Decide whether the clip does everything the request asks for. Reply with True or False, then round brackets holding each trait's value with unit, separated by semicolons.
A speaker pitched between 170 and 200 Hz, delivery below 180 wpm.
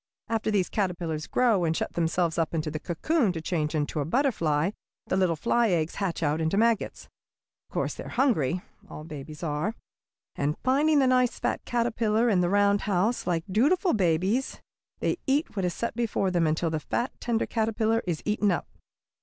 False (190 Hz; 185 wpm)